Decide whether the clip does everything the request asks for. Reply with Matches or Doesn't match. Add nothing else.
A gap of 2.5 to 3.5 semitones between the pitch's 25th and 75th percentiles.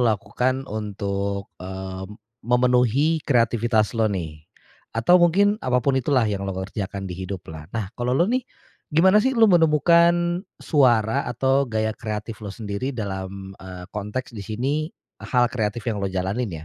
Doesn't match